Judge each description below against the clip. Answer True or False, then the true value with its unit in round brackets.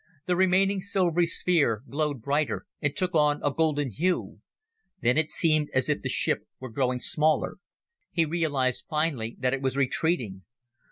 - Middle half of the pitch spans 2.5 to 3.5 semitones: False (4.3 semitones)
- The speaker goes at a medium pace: True (160 wpm)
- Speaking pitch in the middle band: True (150 Hz)